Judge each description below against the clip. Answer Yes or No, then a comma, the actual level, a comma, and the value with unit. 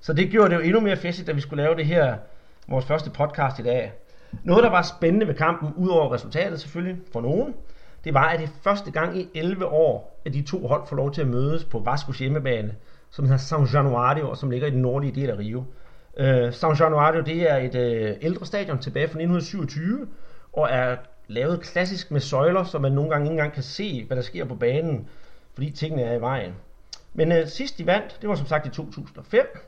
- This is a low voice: No, medium, 155 Hz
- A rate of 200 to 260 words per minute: Yes, fast, 225 wpm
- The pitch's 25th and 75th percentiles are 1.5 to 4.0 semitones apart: No, average, 4.4 semitones